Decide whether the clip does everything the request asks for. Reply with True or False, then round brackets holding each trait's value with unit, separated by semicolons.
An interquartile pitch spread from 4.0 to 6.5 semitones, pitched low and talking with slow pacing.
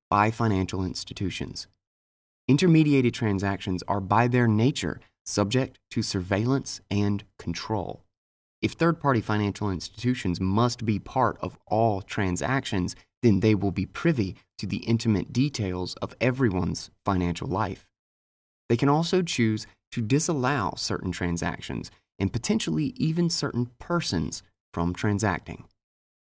True (5.1 semitones; 105 Hz; 120 wpm)